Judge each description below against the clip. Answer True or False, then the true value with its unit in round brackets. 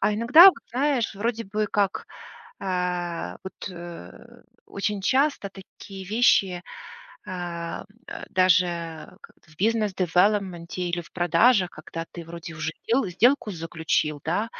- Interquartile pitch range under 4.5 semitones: True (4.0 semitones)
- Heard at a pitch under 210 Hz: True (185 Hz)